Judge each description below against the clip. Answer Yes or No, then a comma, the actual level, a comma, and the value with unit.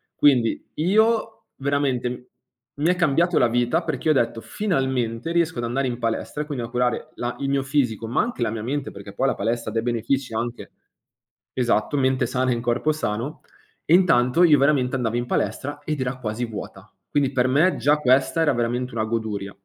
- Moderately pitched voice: No, low, 130 Hz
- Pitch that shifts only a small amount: No, average, 3.7 semitones